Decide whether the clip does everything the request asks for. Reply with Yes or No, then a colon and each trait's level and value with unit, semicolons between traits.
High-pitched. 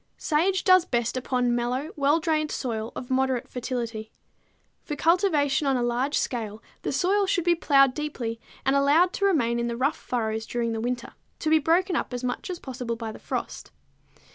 Yes: very high, 265 Hz